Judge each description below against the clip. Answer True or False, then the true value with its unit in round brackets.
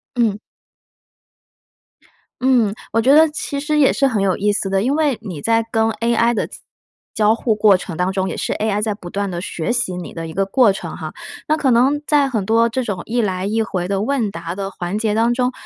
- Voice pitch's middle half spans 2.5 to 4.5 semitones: True (4.0 semitones)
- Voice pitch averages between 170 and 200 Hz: False (220 Hz)